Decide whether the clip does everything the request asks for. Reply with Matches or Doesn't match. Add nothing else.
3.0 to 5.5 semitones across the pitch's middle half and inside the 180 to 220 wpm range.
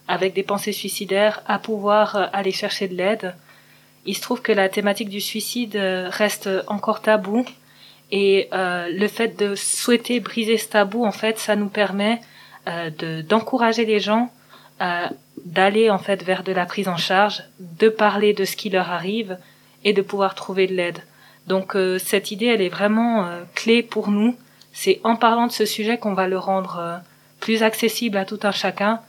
Doesn't match